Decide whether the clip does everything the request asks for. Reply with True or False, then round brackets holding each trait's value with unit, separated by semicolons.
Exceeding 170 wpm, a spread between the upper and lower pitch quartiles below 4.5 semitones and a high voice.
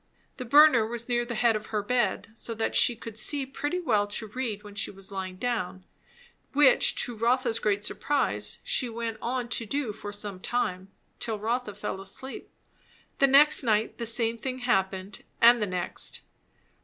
True (180 wpm; 3.3 semitones; 230 Hz)